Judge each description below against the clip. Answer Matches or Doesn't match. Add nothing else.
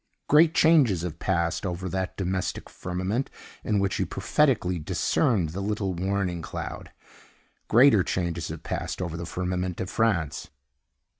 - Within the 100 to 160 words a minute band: Matches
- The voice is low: Matches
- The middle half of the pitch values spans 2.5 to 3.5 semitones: Matches